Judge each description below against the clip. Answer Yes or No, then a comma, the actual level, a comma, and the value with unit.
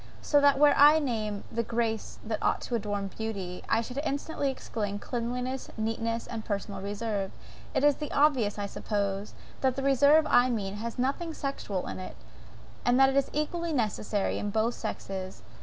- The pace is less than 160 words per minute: No, average, 180 wpm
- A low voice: No, high, 230 Hz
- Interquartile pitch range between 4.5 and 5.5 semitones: Yes, average, 4.8 semitones